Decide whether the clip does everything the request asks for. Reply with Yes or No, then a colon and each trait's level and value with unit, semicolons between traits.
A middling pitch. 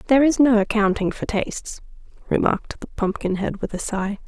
No: high, 215 Hz